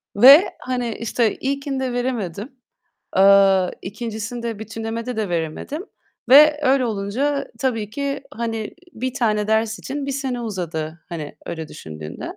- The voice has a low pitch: No, high, 225 Hz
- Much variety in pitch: No, average, 4.8 semitones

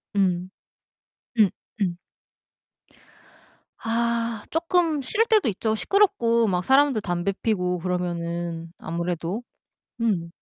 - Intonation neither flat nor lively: Yes, average, 5.0 semitones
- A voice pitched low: No, high, 205 Hz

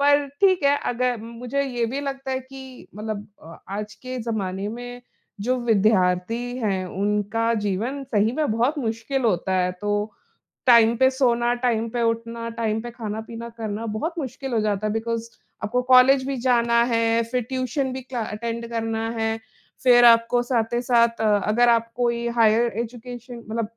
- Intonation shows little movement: Yes, narrow, 2.2 semitones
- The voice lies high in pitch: Yes, high, 235 Hz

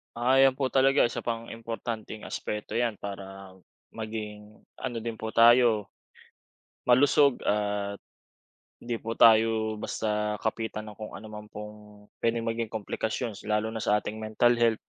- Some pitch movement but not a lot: No, narrow, 1.8 semitones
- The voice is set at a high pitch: No, low, 110 Hz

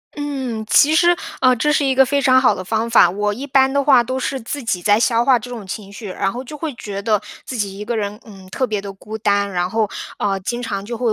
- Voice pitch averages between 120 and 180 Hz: No, high, 230 Hz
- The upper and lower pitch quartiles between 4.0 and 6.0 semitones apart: Yes, average, 4.4 semitones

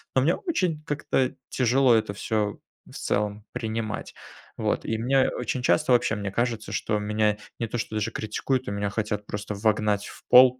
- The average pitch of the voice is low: Yes, low, 110 Hz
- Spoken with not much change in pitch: No, average, 3.5 semitones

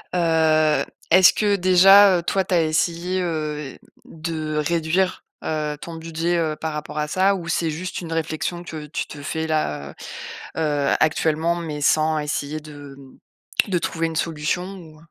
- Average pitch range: No, narrow, 2.2 semitones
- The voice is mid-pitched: Yes, medium, 160 Hz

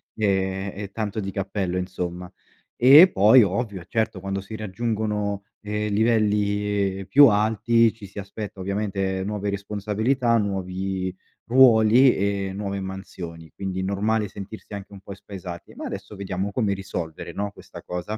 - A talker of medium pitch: No, low, 100 Hz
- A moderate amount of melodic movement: No, narrow, 2.0 semitones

